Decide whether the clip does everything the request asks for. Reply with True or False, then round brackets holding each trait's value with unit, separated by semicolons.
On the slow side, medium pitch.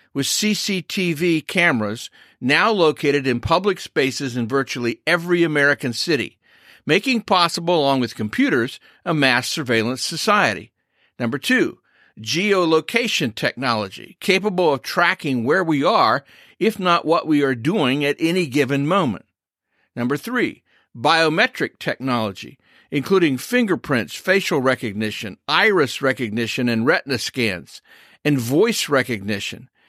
True (115 wpm; 145 Hz)